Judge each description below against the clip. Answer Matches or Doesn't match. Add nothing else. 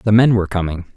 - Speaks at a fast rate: Matches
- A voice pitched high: Doesn't match